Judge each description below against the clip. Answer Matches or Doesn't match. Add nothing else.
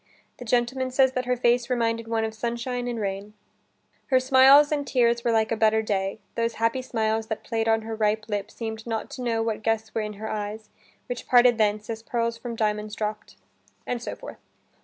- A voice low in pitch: Doesn't match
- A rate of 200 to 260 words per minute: Matches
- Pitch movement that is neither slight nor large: Doesn't match